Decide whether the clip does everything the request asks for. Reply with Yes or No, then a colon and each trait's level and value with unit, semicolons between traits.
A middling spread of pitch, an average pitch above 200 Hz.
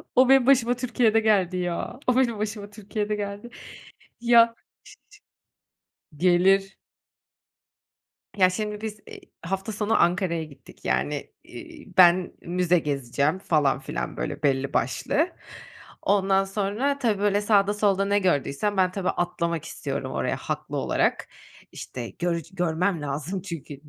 No: average, 3.7 semitones; high, 195 Hz